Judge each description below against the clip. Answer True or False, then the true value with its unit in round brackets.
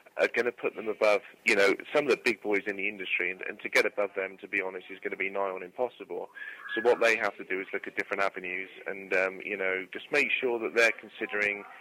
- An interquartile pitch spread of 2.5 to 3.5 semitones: True (2.9 semitones)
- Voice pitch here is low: True (100 Hz)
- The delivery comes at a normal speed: False (270 wpm)